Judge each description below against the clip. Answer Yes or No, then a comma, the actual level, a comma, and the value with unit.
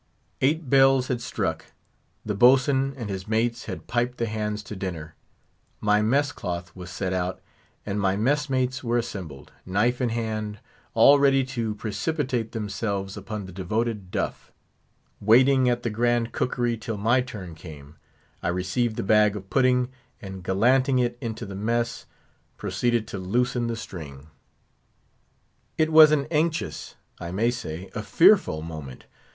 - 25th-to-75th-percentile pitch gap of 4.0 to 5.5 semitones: Yes, average, 4.6 semitones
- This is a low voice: Yes, low, 110 Hz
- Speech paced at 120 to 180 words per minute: Yes, average, 150 wpm